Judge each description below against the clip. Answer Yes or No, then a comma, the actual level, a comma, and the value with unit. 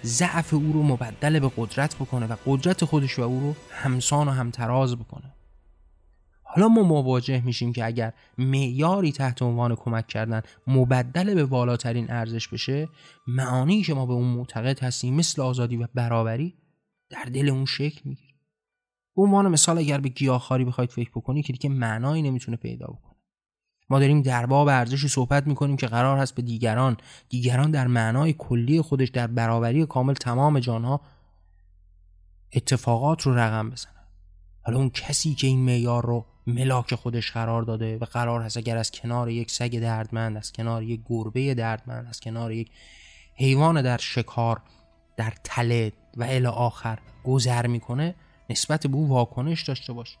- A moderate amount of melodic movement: Yes, average, 3.2 semitones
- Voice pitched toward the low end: Yes, low, 125 Hz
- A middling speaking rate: No, fast, 160 wpm